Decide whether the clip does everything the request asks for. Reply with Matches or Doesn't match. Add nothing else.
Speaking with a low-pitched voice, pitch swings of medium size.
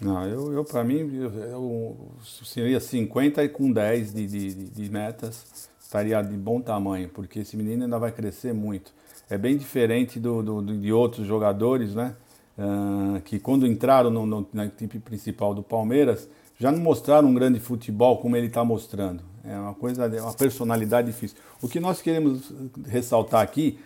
Matches